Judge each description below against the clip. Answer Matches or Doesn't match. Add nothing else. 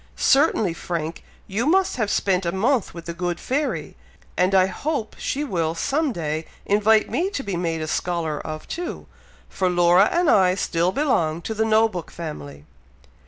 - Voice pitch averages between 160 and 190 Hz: Matches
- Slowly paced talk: Doesn't match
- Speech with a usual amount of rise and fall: Doesn't match